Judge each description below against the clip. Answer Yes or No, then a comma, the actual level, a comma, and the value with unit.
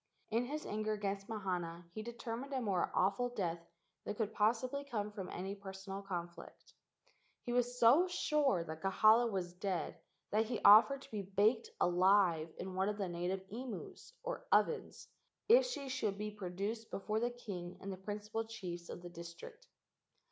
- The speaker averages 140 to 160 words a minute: No, average, 170 wpm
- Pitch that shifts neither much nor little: Yes, average, 4.1 semitones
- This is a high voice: Yes, high, 205 Hz